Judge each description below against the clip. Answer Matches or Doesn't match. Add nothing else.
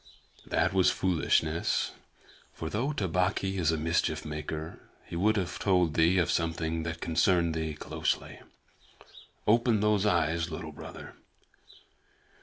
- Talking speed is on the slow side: Matches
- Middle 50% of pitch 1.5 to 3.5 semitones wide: Matches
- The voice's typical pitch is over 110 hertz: Doesn't match